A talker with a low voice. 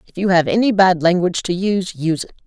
No: medium, 185 Hz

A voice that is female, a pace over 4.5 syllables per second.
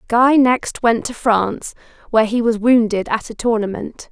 Yes: female; 4.8 syllables/s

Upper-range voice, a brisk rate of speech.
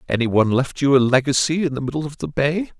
No: medium, 140 Hz; fast, 255 wpm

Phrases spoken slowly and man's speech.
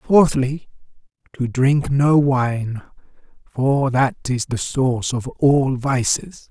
Yes: slow, 120 wpm; male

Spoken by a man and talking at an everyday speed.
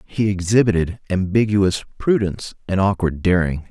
No: male; slow, 115 wpm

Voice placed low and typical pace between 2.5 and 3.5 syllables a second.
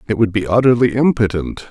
No: low, 110 Hz; 5.8 syllables/s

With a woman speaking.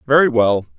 No: male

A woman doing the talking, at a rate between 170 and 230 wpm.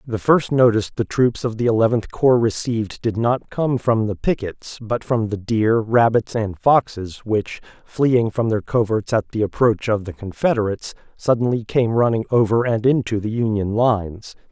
No: male; average, 180 wpm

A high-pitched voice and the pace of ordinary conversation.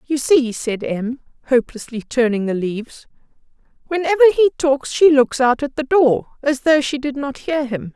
Yes: very high, 270 Hz; average, 180 wpm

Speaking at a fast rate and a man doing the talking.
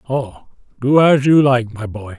No: average, 190 wpm; male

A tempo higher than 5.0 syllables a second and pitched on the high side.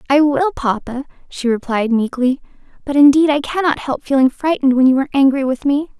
Yes: 5.9 syllables/s; very high, 275 Hz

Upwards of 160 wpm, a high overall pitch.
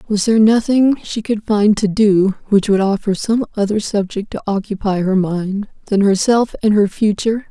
Yes: average, 185 wpm; high, 205 Hz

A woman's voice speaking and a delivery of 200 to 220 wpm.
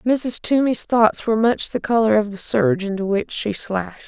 Yes: female; fast, 205 wpm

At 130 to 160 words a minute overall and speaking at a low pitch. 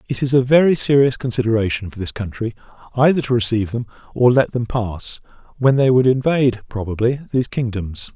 No: average, 175 wpm; low, 120 Hz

